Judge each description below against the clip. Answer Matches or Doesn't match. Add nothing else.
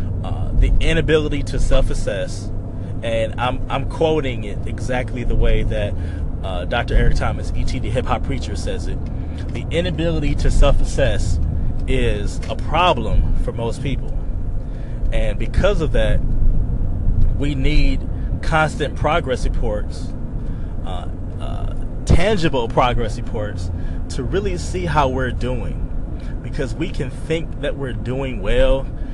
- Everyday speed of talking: Doesn't match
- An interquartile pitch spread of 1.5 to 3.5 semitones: Doesn't match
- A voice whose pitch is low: Matches